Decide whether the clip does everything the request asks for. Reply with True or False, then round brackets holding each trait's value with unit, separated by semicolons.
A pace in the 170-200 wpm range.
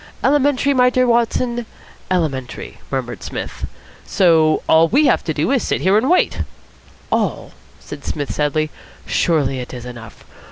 False (155 wpm)